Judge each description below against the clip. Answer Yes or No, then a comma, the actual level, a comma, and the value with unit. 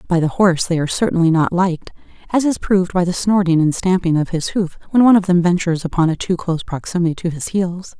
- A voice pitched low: No, medium, 175 Hz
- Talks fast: Yes, fast, 240 wpm